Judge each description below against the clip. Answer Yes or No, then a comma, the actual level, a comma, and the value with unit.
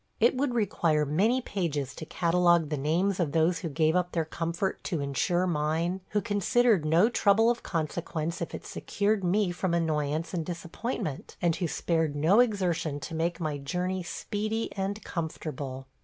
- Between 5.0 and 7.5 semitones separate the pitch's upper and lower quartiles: No, average, 3.8 semitones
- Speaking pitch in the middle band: Yes, medium, 170 Hz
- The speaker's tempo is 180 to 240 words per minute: No, average, 170 wpm